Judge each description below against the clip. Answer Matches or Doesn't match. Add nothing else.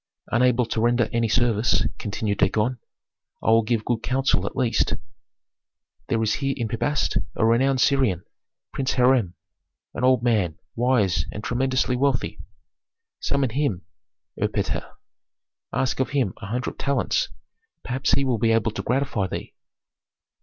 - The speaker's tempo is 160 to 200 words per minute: Doesn't match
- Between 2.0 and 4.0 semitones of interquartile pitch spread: Matches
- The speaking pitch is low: Matches